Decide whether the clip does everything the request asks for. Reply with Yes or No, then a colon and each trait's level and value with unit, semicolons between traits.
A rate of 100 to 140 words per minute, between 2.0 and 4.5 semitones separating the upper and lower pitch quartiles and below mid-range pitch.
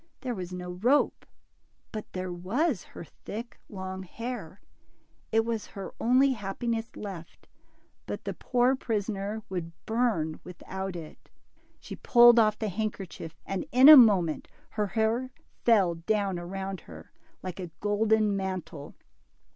No: slow, 135 wpm; average, 3.9 semitones; high, 205 Hz